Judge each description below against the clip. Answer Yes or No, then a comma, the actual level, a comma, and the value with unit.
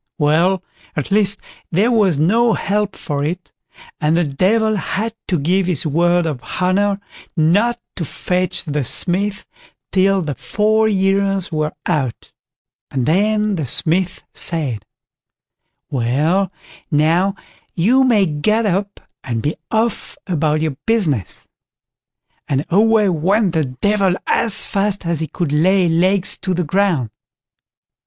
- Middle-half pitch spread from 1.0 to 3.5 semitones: No, average, 4.5 semitones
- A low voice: No, medium, 185 Hz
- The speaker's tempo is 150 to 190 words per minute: No, slow, 135 wpm